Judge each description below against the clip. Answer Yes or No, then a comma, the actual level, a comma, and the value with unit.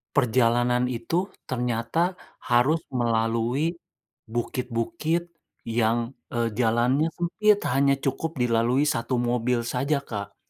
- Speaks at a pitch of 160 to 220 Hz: No, low, 125 Hz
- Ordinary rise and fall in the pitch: Yes, average, 3.7 semitones